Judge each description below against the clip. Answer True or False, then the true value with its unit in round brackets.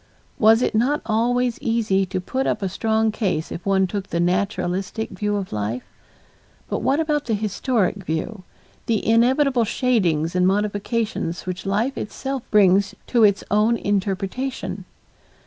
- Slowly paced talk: False (145 wpm)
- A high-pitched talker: True (210 Hz)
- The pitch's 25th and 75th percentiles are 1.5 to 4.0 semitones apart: True (3.7 semitones)